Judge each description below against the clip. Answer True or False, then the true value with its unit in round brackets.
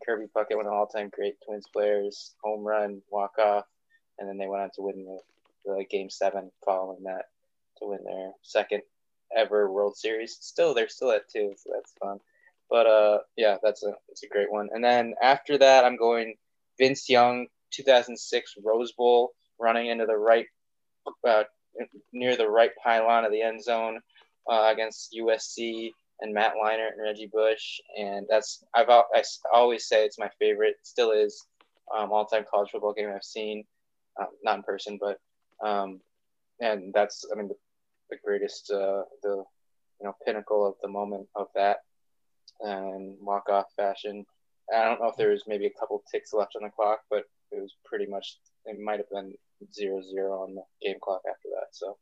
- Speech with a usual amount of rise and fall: True (3.2 semitones)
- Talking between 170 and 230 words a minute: True (185 wpm)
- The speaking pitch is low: True (110 Hz)